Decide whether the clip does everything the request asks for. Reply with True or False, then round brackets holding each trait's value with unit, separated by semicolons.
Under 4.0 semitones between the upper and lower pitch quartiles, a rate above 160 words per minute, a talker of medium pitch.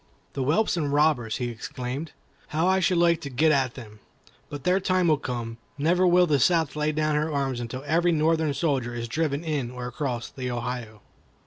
False (4.7 semitones; 200 wpm; 145 Hz)